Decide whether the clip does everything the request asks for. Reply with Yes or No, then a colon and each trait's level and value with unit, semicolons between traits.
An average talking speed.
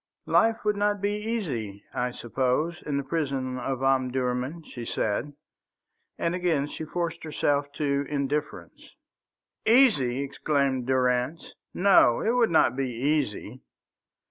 No: slow, 125 wpm